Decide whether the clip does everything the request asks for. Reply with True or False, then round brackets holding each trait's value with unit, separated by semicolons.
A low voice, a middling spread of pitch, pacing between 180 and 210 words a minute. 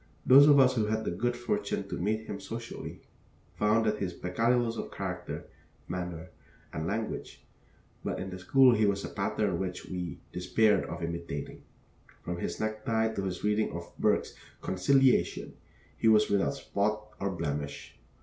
False (105 Hz; 3.7 semitones; 170 wpm)